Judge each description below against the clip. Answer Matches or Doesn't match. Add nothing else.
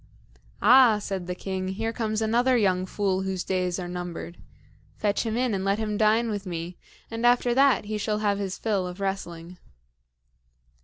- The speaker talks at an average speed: Matches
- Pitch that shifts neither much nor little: Matches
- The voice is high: Matches